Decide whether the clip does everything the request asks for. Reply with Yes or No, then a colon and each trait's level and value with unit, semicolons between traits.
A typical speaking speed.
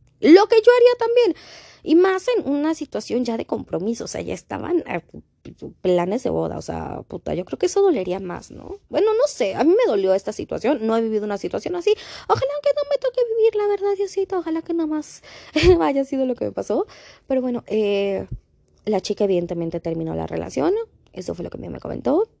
No: fast, 220 wpm